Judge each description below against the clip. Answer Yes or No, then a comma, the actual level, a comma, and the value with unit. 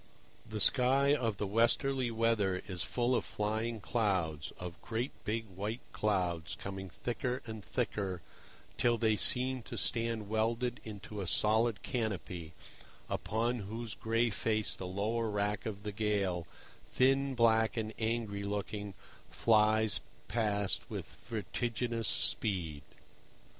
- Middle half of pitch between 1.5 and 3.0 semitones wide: Yes, narrow, 2.6 semitones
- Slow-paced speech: Yes, slow, 125 wpm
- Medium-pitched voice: No, low, 110 Hz